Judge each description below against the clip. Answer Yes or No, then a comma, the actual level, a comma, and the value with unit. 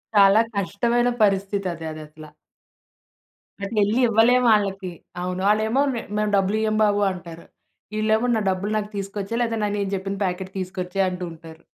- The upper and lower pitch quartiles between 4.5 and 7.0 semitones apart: No, average, 2.7 semitones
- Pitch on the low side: No, high, 200 Hz